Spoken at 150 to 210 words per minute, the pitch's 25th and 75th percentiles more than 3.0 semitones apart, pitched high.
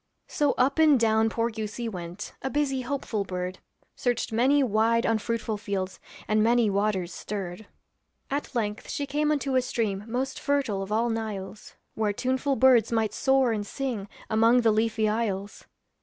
Yes: average, 160 wpm; average, 3.8 semitones; high, 225 Hz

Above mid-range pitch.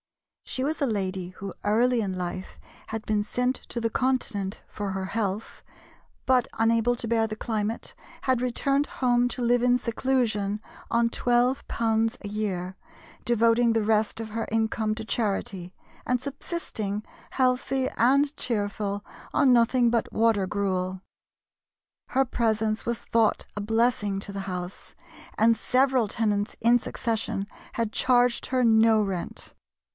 Yes: high, 225 Hz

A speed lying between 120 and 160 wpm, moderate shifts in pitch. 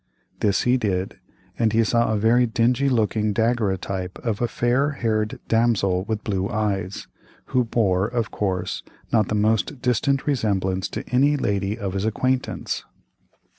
Yes: average, 150 wpm; average, 3.5 semitones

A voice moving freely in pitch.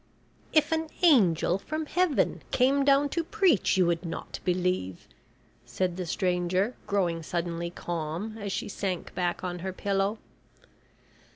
Yes: wide, 7.4 semitones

